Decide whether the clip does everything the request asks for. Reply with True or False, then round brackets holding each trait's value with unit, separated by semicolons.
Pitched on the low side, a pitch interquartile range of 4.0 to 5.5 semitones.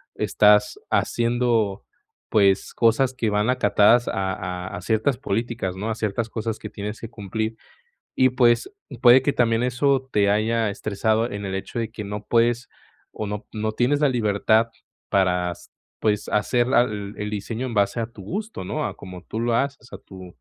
False (110 Hz; 2.9 semitones)